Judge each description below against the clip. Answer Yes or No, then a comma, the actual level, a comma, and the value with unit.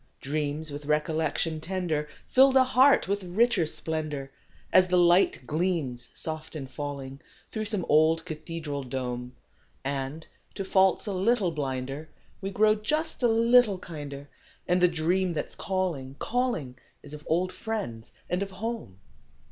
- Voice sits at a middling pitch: Yes, medium, 165 Hz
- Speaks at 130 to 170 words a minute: Yes, average, 150 wpm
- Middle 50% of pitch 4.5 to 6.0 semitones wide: Yes, average, 5.2 semitones